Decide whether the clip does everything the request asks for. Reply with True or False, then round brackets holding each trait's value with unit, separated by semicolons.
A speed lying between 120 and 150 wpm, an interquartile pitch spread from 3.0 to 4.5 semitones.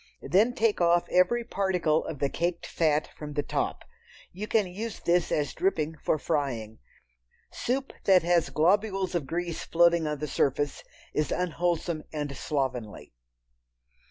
True (145 wpm; 3.7 semitones)